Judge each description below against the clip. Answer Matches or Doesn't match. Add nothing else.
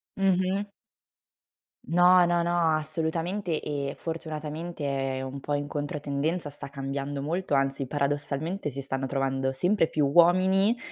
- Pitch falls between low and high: Matches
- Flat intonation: Doesn't match